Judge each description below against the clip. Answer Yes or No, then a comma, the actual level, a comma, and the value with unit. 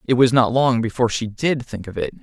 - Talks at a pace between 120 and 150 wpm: No, fast, 270 wpm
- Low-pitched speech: Yes, low, 120 Hz